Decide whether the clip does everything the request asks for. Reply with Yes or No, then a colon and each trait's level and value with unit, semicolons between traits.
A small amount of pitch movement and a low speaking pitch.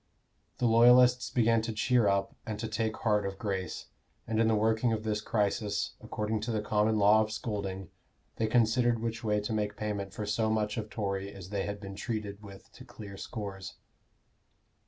Yes: narrow, 1.7 semitones; low, 105 Hz